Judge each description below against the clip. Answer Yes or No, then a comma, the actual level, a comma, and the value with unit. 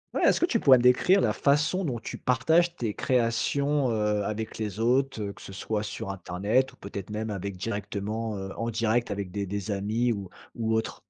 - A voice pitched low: Yes, low, 110 Hz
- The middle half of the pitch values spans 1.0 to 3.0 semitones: No, average, 3.7 semitones